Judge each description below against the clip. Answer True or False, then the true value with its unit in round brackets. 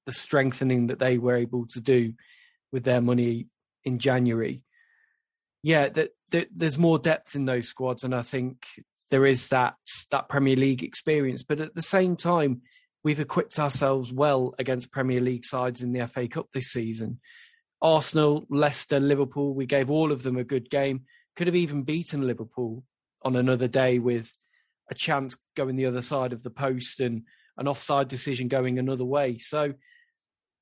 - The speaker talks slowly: False (170 wpm)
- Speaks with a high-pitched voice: False (135 Hz)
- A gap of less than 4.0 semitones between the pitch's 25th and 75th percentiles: True (3.1 semitones)